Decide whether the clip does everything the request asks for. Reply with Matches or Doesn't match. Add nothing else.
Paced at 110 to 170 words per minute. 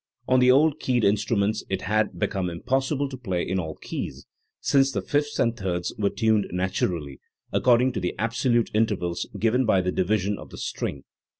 Doesn't match